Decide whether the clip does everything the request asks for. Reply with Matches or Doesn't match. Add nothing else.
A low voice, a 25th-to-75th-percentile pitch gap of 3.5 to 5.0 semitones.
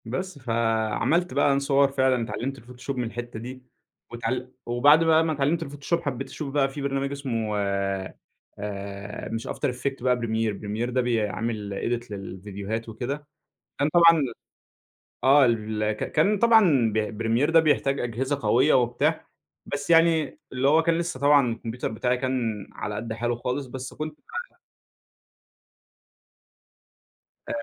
Matches